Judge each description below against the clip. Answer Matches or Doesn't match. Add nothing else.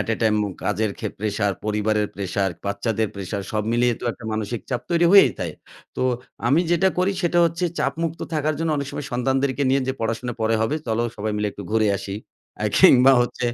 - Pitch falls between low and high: Doesn't match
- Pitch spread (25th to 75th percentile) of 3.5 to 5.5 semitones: Matches